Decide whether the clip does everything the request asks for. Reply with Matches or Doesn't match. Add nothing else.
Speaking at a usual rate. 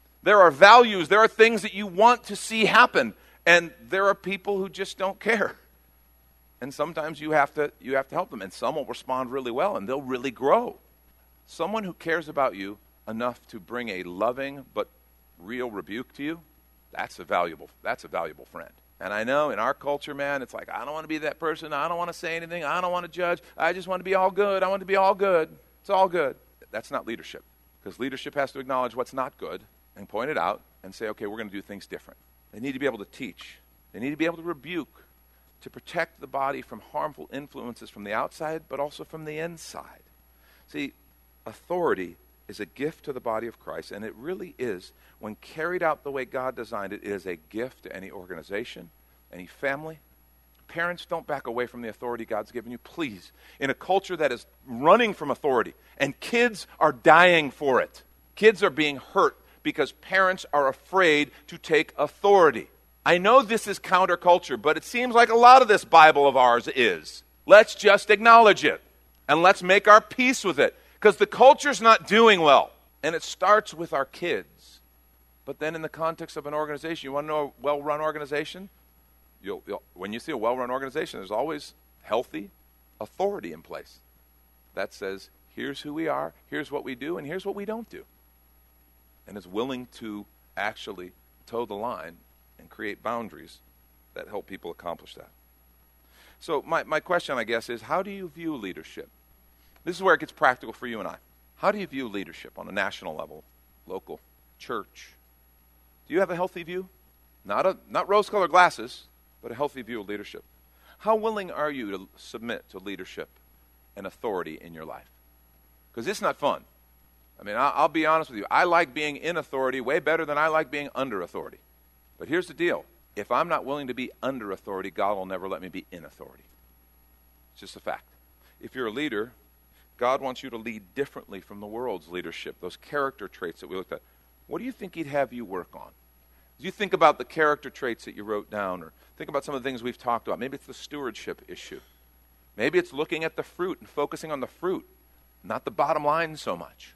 Doesn't match